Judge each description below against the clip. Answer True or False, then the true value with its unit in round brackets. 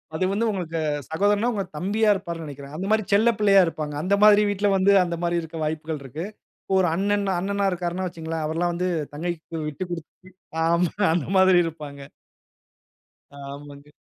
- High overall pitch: False (175 Hz)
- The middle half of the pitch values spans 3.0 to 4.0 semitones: True (3.7 semitones)